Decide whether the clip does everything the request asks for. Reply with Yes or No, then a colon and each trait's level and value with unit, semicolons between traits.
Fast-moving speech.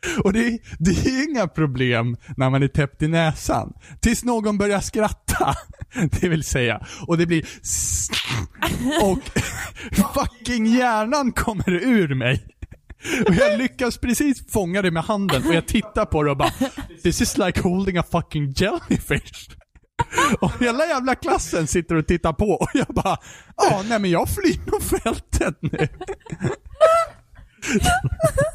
No: average, 145 wpm